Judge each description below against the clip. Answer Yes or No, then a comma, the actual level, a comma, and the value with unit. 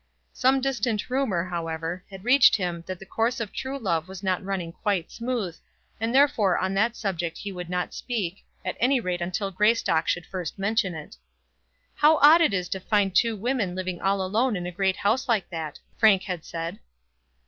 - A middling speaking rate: Yes, average, 190 wpm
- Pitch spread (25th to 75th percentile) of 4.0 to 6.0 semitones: Yes, average, 4.6 semitones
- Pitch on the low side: No, high, 195 Hz